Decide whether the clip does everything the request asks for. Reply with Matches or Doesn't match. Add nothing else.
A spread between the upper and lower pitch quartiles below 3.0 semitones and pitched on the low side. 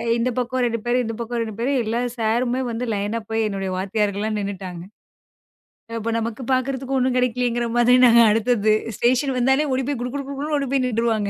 Doesn't match